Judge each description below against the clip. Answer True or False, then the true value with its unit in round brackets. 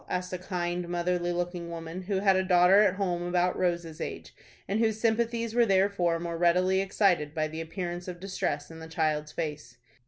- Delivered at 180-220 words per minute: True (190 wpm)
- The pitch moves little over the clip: True (2.2 semitones)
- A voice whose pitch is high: False (175 Hz)